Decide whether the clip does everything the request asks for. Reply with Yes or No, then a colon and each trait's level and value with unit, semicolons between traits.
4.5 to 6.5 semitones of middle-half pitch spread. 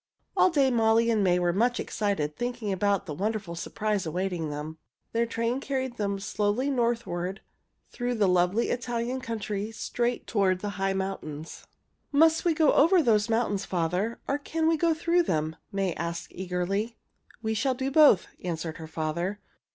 Yes: average, 5.2 semitones